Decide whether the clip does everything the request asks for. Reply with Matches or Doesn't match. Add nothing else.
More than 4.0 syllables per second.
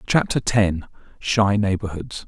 Doesn't match